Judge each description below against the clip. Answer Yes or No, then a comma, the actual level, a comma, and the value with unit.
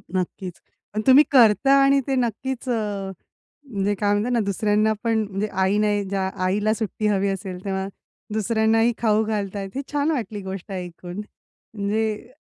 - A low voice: No, high, 210 Hz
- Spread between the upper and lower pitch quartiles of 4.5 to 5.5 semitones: No, narrow, 2.5 semitones